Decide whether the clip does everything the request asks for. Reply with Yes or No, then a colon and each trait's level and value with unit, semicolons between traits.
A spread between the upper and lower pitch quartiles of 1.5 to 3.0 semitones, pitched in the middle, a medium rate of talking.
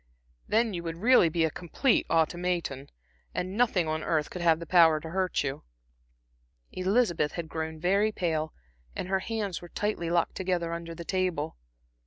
Yes: average, 2.7 semitones; medium, 170 Hz; average, 165 wpm